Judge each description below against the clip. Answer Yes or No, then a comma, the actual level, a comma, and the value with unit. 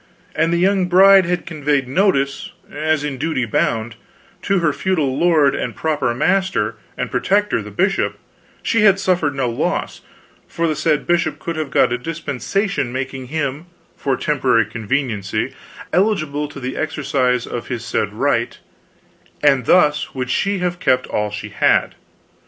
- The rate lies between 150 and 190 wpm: Yes, average, 155 wpm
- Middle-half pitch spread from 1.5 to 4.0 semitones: No, average, 5.3 semitones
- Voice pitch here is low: No, medium, 150 Hz